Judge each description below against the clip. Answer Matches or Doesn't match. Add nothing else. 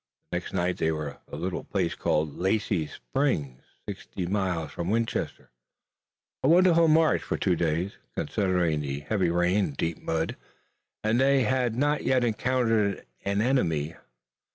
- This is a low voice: Matches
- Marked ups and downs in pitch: Matches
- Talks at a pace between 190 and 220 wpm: Doesn't match